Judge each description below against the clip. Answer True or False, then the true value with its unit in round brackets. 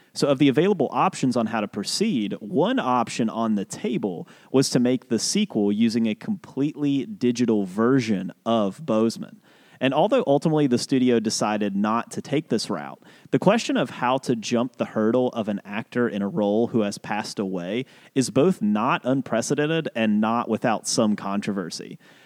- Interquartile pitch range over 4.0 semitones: True (4.4 semitones)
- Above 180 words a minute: False (175 wpm)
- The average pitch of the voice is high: False (120 Hz)